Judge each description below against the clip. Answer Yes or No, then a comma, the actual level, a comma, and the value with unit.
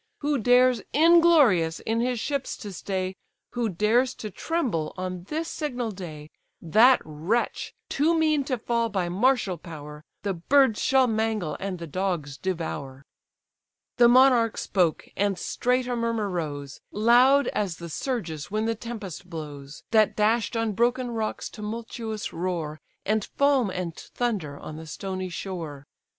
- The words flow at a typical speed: Yes, average, 145 wpm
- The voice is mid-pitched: No, high, 210 Hz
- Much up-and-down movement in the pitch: Yes, wide, 6.0 semitones